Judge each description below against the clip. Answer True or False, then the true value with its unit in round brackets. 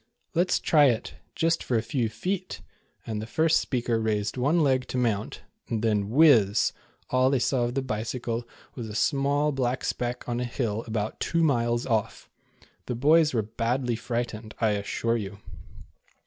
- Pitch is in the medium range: False (120 Hz)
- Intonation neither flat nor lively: True (3.5 semitones)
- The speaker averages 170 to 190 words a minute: True (175 wpm)